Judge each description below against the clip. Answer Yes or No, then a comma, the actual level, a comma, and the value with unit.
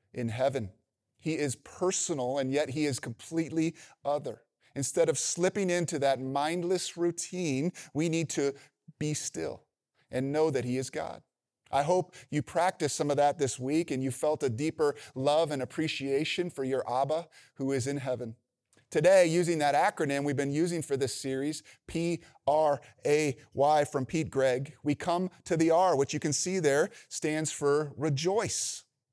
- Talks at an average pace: Yes, average, 170 wpm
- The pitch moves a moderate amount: Yes, average, 3.2 semitones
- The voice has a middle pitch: Yes, medium, 150 Hz